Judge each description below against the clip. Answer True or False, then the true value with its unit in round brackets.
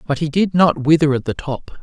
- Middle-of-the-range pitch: True (155 Hz)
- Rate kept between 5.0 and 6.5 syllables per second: True (5.4 syllables/s)